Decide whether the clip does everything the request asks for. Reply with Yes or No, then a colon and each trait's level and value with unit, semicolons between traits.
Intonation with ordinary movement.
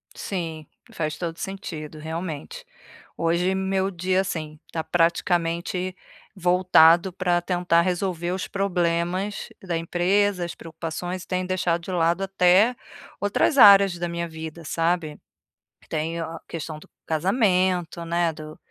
No: narrow, 2.1 semitones